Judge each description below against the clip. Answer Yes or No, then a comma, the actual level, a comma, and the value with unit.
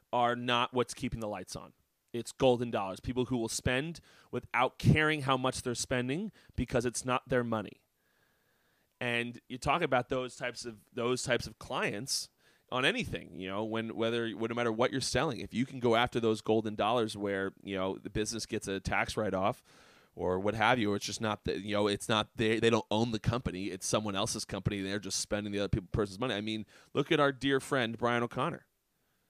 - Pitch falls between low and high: No, low, 115 Hz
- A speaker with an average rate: No, fast, 220 wpm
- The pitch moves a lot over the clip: No, average, 3.0 semitones